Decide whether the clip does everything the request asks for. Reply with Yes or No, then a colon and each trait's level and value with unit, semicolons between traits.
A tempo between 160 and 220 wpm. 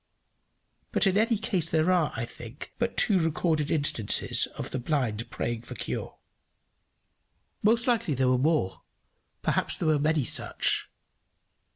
No: average, 145 wpm